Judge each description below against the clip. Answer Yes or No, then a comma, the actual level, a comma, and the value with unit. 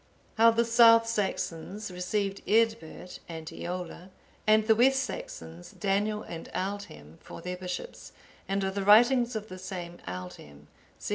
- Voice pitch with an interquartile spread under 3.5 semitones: No, average, 4.2 semitones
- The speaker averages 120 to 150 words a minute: Yes, average, 140 wpm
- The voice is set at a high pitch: Yes, high, 195 Hz